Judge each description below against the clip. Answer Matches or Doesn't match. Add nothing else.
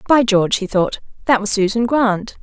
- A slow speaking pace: Doesn't match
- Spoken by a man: Doesn't match